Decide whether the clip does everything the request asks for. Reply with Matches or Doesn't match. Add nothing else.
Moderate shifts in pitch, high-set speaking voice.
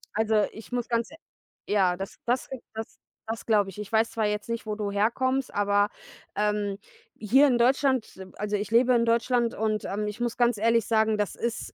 Doesn't match